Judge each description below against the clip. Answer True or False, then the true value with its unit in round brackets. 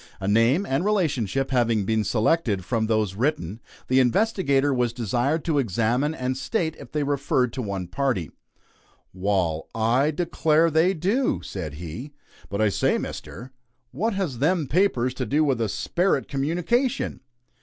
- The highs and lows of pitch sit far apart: True (6.3 semitones)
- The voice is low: True (130 Hz)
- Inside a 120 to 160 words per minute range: True (155 wpm)